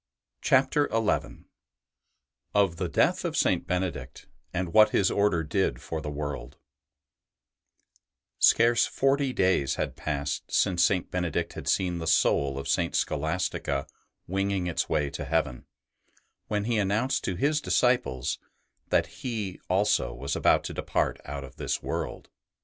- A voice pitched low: Yes, very low, 90 Hz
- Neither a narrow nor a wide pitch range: No, wide, 6.3 semitones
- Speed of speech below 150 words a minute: Yes, average, 140 wpm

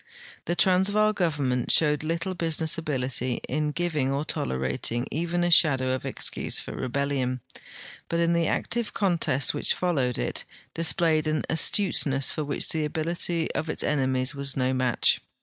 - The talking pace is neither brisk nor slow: Yes, average, 150 wpm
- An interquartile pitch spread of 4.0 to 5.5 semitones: Yes, average, 4.4 semitones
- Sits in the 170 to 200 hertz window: No, medium, 155 Hz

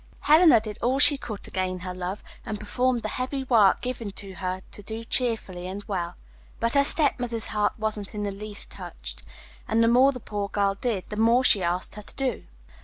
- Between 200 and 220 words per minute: Yes, fast, 205 wpm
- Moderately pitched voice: No, high, 215 Hz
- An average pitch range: Yes, average, 4.0 semitones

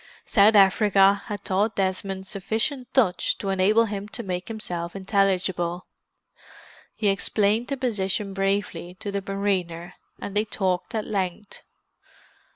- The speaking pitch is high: Yes, high, 195 Hz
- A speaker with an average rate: No, slow, 130 wpm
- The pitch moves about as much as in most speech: No, narrow, 1.9 semitones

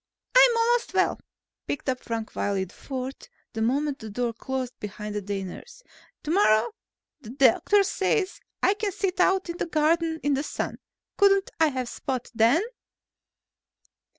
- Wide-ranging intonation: Yes, wide, 8.8 semitones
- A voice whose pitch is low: No, very high, 275 Hz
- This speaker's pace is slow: No, average, 150 wpm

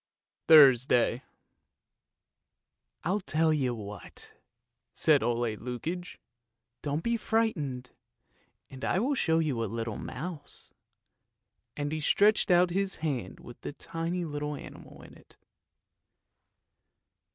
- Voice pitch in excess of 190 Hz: No, medium, 145 Hz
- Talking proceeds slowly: Yes, slow, 120 wpm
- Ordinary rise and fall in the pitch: No, wide, 6.1 semitones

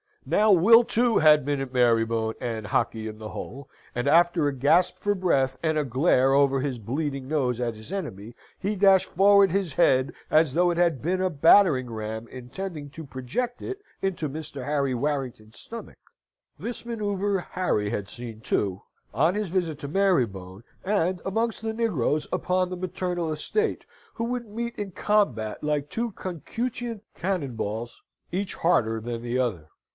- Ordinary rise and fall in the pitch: No, wide, 7.7 semitones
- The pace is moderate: Yes, average, 170 wpm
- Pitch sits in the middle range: Yes, medium, 150 Hz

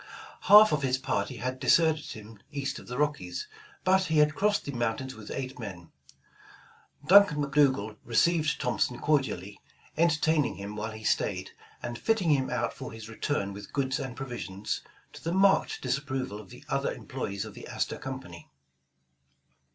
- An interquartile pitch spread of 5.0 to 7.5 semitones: Yes, wide, 5.5 semitones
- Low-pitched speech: Yes, low, 130 Hz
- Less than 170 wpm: Yes, average, 160 wpm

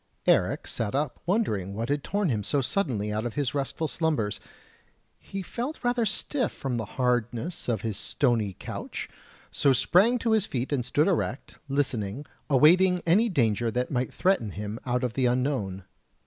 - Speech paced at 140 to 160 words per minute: No, average, 170 wpm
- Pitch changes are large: Yes, wide, 7.6 semitones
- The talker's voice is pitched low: Yes, low, 130 Hz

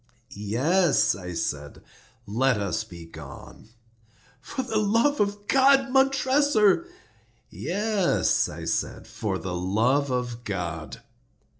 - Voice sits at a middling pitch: No, low, 130 Hz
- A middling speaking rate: No, slow, 110 wpm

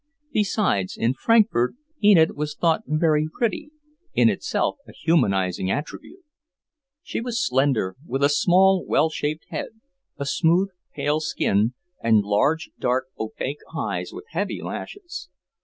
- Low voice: No, medium, 150 Hz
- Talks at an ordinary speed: No, slow, 130 wpm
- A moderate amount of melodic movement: No, wide, 7.3 semitones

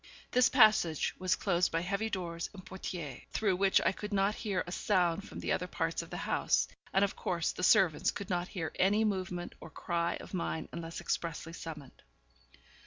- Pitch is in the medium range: Yes, medium, 180 Hz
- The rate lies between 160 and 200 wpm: Yes, average, 190 wpm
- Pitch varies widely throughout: No, average, 2.8 semitones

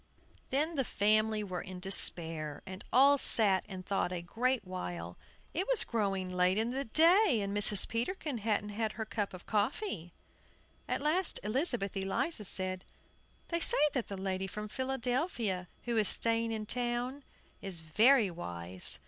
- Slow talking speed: No, average, 155 wpm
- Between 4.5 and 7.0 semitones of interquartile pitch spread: Yes, average, 5.1 semitones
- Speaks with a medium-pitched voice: No, high, 215 Hz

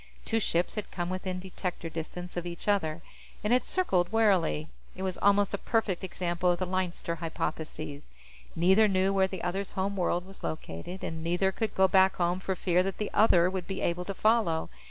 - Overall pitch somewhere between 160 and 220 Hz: Yes, medium, 185 Hz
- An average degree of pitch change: No, narrow, 2.1 semitones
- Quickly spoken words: No, average, 195 wpm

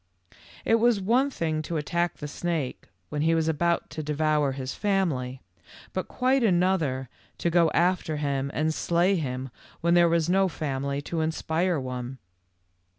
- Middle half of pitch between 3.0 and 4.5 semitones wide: Yes, average, 3.6 semitones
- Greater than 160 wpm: No, average, 155 wpm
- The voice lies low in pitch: No, medium, 160 Hz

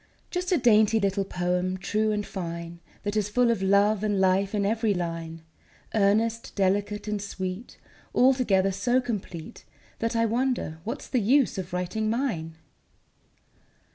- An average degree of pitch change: Yes, average, 3.5 semitones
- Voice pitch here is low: No, high, 205 Hz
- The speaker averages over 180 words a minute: No, average, 145 wpm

